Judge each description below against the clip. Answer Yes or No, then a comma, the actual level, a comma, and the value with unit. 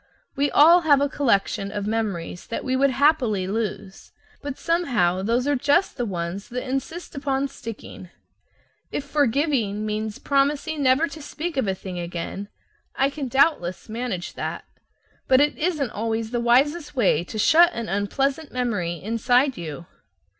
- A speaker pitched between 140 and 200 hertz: No, very high, 250 Hz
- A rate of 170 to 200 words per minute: No, average, 155 wpm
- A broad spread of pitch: Yes, wide, 5.8 semitones